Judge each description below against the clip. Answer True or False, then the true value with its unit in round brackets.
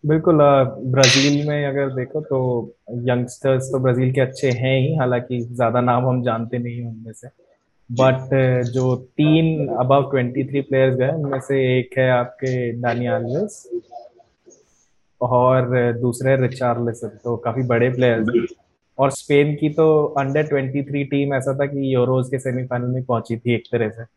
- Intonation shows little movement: True (2.1 semitones)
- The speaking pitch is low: True (130 Hz)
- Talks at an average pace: True (155 wpm)